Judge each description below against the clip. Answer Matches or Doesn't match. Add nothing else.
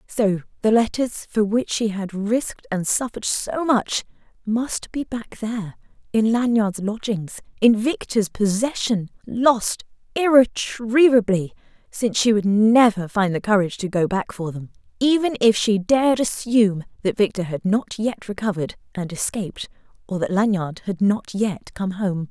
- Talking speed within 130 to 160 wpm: Matches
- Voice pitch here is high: Matches